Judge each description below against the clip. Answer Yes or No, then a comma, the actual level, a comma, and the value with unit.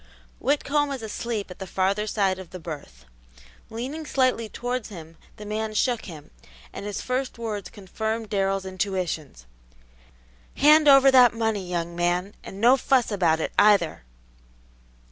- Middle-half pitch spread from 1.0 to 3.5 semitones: No, average, 4.7 semitones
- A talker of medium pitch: No, high, 210 Hz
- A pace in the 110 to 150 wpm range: Yes, average, 145 wpm